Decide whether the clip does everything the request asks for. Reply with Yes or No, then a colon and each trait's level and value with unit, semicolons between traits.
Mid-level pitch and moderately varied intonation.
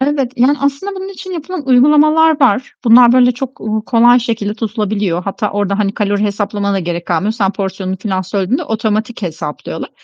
No: high, 220 Hz; average, 4.6 semitones